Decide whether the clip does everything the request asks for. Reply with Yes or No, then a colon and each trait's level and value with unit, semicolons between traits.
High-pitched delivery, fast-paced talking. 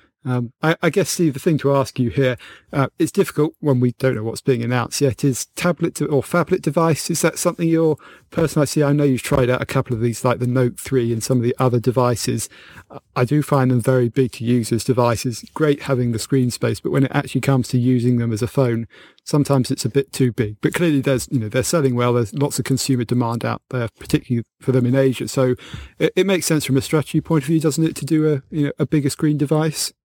No: low, 135 Hz; fast, 255 wpm